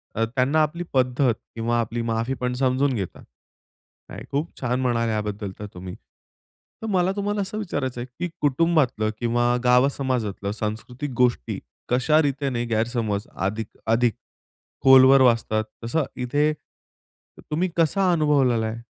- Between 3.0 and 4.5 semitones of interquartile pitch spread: Yes, average, 4.1 semitones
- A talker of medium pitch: No, low, 125 Hz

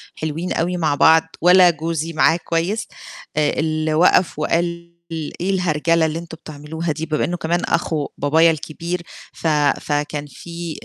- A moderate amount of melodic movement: No, narrow, 1.7 semitones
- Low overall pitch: No, medium, 165 Hz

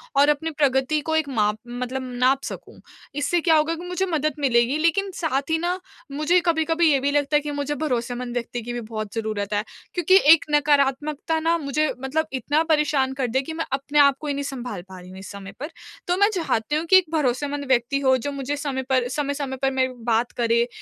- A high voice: Yes, very high, 280 Hz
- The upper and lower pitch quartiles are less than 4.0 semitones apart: Yes, average, 3.6 semitones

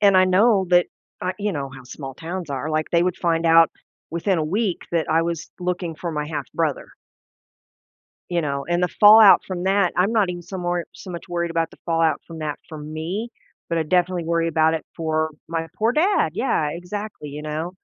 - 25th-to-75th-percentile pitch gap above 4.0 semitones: No, average, 2.7 semitones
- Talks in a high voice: No, medium, 170 Hz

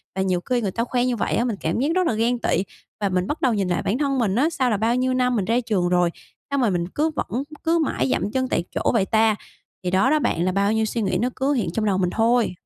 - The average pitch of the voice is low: No, high, 225 Hz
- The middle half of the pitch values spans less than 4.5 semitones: No, average, 4.8 semitones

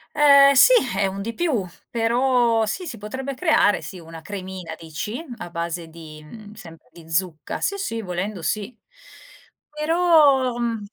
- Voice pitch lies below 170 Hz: No, high, 215 Hz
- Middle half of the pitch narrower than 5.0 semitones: No, wide, 7.2 semitones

